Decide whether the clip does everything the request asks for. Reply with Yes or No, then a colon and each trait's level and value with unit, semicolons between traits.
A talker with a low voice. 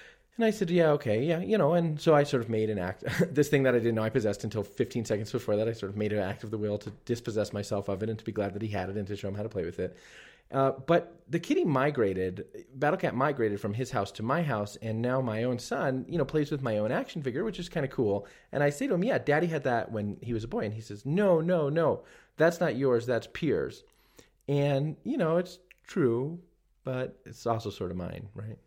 Yes: low, 120 Hz